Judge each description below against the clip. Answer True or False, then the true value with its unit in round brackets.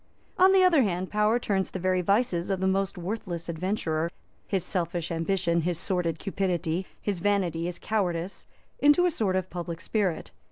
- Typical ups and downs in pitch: True (3.1 semitones)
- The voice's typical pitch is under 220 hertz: True (185 Hz)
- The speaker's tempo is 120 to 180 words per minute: True (170 wpm)